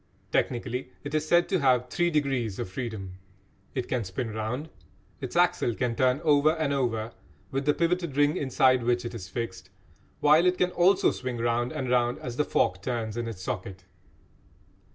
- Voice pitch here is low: Yes, low, 125 Hz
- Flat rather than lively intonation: No, average, 4.2 semitones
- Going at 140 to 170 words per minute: No, average, 180 wpm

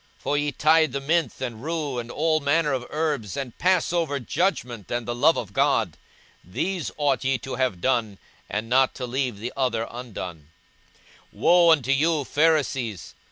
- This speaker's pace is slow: No, average, 170 wpm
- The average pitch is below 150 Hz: Yes, low, 135 Hz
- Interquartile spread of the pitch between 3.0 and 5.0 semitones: Yes, average, 4.6 semitones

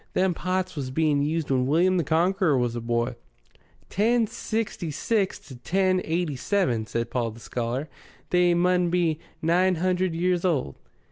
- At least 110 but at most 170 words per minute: Yes, average, 160 wpm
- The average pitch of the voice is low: No, medium, 170 Hz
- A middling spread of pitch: No, wide, 5.7 semitones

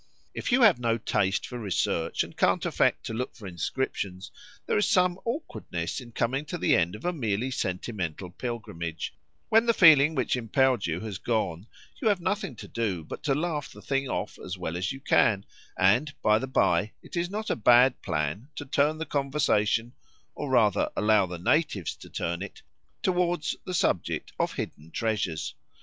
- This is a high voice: No, low, 115 Hz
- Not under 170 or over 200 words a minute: Yes, average, 185 wpm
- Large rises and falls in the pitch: Yes, wide, 7.8 semitones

